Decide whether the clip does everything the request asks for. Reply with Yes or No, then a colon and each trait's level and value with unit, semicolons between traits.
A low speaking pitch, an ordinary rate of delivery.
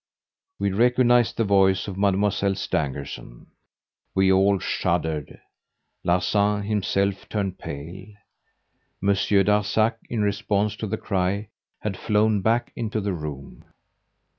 No: low, 100 Hz; slow, 115 wpm